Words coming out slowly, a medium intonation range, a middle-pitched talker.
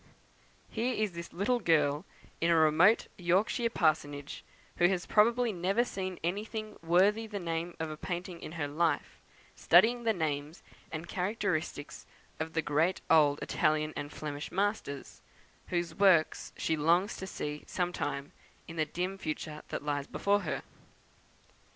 No: average, 150 wpm; average, 4.5 semitones; medium, 170 Hz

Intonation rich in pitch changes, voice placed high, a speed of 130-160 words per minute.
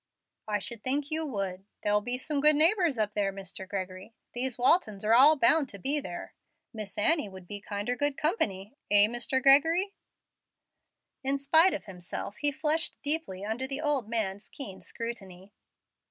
No: wide, 6.3 semitones; high, 240 Hz; average, 170 wpm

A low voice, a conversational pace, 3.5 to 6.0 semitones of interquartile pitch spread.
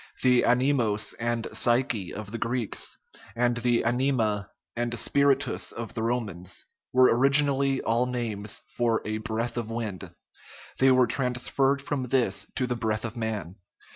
No: low, 120 Hz; average, 165 wpm; narrow, 2.6 semitones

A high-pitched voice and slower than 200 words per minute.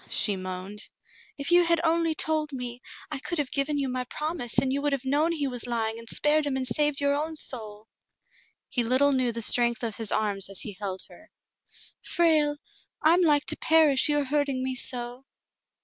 No: very high, 270 Hz; fast, 205 wpm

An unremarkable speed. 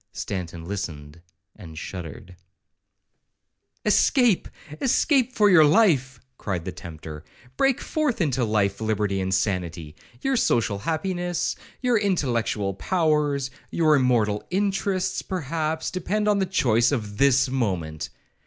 No: slow, 115 wpm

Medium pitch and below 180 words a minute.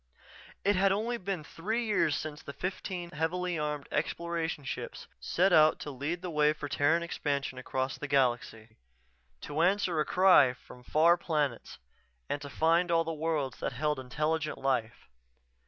Yes: medium, 155 Hz; average, 160 wpm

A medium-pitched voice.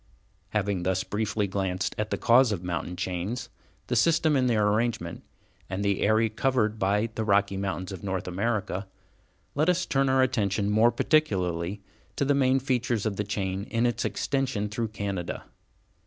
No: low, 105 Hz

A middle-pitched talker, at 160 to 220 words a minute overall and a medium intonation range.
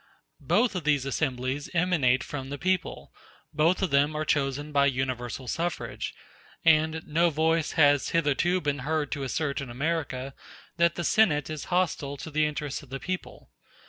Yes: medium, 150 Hz; average, 165 wpm; average, 3.1 semitones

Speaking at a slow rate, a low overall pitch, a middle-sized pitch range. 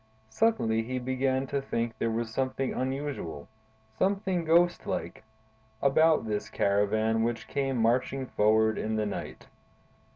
Yes: slow, 130 wpm; low, 125 Hz; average, 3.8 semitones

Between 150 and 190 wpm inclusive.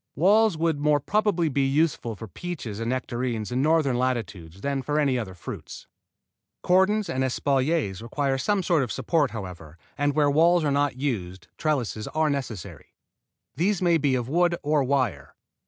Yes: average, 165 wpm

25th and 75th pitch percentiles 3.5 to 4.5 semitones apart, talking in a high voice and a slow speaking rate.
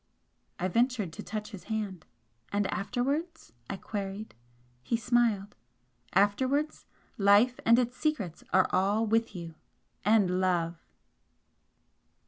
Yes: average, 4.0 semitones; high, 210 Hz; slow, 110 wpm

